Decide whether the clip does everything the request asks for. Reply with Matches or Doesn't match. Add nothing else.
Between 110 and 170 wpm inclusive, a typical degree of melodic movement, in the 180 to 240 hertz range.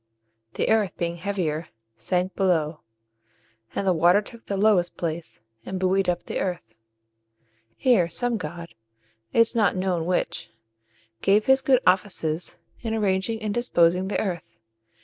Matches